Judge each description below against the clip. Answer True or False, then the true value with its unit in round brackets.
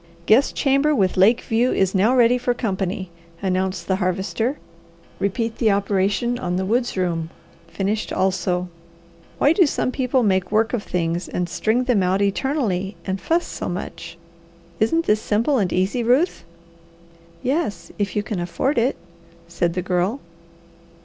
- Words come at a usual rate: True (155 wpm)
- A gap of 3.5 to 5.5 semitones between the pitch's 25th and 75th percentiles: True (4.7 semitones)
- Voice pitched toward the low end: False (205 Hz)